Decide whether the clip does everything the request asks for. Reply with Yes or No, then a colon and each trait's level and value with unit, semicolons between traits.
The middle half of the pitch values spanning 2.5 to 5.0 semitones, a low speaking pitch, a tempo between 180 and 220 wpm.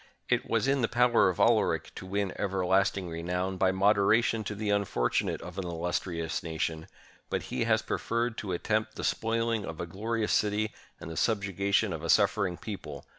Yes: average, 3.6 semitones; low, 100 Hz; average, 185 wpm